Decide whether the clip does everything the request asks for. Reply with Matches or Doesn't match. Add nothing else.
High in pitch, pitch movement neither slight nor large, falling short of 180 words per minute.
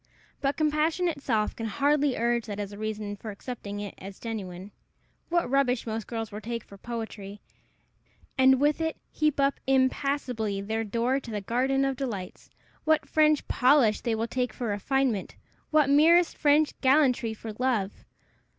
Matches